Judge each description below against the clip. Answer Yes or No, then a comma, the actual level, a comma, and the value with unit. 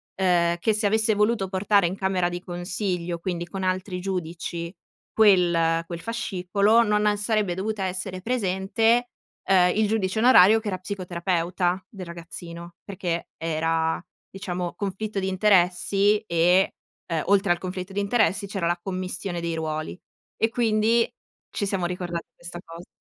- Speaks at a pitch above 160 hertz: Yes, medium, 185 Hz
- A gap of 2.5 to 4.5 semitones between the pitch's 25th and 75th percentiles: Yes, average, 2.8 semitones